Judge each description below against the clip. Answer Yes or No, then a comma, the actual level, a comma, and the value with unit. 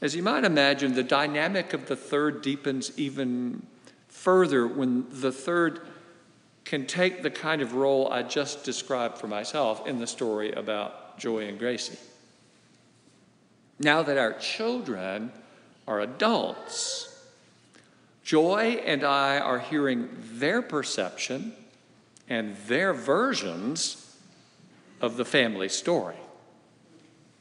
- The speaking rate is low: Yes, slow, 115 wpm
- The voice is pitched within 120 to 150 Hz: Yes, medium, 140 Hz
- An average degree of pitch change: Yes, average, 4.8 semitones